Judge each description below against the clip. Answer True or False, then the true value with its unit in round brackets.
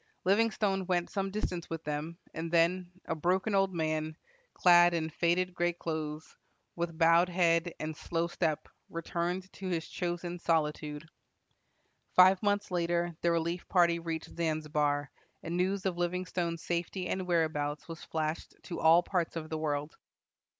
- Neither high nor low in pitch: True (170 Hz)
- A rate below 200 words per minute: True (150 wpm)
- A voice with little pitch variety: True (2.0 semitones)